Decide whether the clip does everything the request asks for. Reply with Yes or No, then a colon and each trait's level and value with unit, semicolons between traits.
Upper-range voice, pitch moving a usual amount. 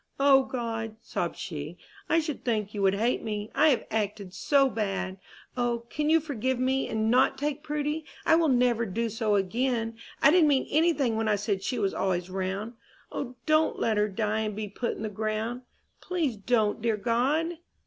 Yes: high, 230 Hz; average, 4.5 semitones